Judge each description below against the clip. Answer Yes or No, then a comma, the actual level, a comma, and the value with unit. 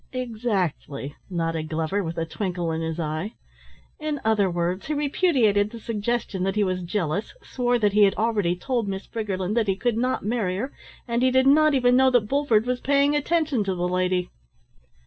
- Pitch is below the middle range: No, high, 210 Hz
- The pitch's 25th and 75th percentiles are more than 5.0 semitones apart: Yes, wide, 5.4 semitones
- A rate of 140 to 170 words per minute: No, average, 190 wpm